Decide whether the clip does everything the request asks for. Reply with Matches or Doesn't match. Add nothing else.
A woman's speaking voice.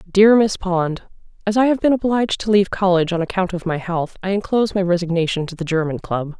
Matches